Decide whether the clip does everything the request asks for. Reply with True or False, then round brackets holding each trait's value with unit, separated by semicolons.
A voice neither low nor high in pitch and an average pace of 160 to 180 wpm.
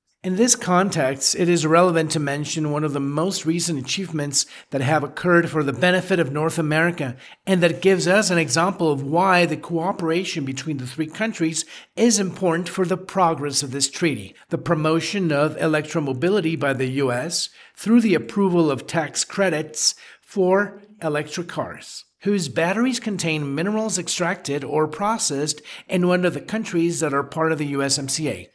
True (165 Hz; 165 wpm)